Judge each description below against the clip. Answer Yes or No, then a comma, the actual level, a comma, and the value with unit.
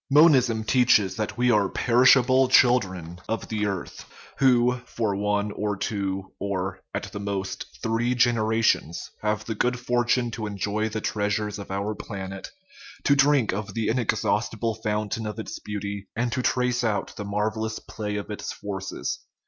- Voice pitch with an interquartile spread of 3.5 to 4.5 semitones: No, average, 3.0 semitones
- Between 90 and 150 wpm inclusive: No, average, 165 wpm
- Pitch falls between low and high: No, low, 110 Hz